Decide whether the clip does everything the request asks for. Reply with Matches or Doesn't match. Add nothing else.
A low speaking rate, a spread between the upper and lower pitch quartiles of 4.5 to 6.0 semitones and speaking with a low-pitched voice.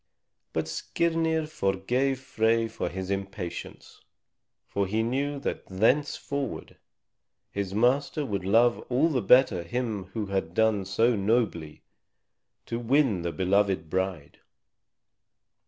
Matches